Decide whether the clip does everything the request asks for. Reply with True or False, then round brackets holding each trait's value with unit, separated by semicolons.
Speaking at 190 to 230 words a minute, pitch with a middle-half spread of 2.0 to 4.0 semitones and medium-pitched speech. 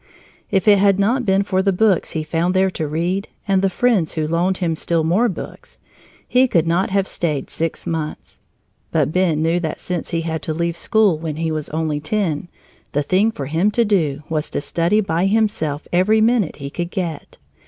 True (205 wpm; 3.7 semitones; 175 Hz)